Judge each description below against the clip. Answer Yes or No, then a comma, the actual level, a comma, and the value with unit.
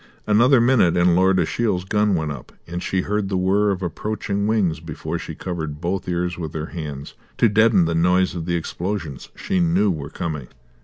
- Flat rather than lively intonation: No, average, 3.7 semitones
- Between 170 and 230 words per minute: Yes, average, 190 wpm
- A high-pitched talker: No, very low, 90 Hz